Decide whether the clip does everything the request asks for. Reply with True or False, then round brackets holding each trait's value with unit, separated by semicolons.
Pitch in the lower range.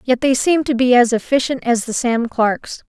False (250 Hz)